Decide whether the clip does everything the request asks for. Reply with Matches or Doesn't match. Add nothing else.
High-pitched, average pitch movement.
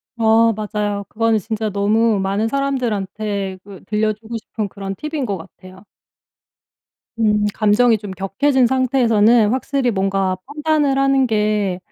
Matches